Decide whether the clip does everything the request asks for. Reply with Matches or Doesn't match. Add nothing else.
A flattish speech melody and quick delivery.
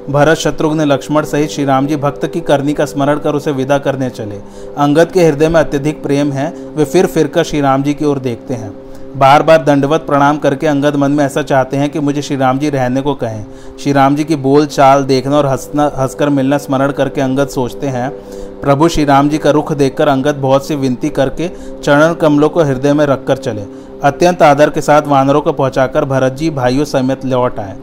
Matches